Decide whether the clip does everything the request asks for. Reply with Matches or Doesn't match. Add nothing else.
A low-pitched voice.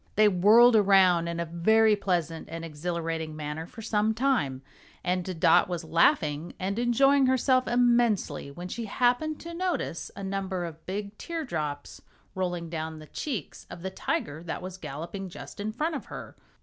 Doesn't match